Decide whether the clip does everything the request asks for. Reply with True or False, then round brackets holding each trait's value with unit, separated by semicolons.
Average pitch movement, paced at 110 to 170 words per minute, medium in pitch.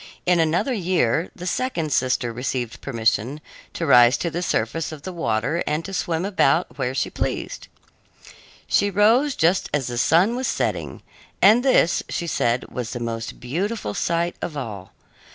False (6.7 semitones; 165 wpm; 160 Hz)